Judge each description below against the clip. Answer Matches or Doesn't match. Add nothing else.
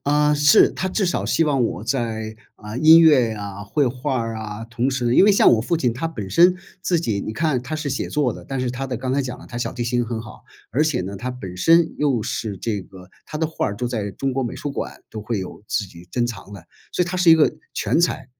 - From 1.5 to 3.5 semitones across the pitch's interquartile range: Doesn't match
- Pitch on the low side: Matches